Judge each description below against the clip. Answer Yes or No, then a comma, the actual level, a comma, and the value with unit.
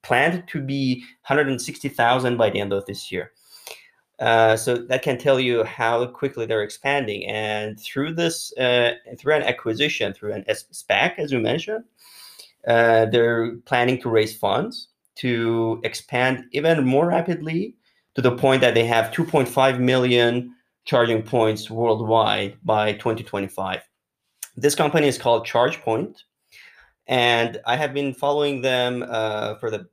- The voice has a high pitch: No, low, 120 Hz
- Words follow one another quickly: No, average, 140 wpm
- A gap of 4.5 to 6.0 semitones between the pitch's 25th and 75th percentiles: No, average, 3.7 semitones